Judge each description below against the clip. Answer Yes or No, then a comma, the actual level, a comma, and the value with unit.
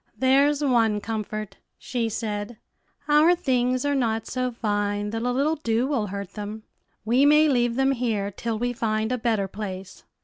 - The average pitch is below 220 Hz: No, high, 230 Hz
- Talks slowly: No, average, 170 wpm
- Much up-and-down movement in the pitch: No, average, 3.6 semitones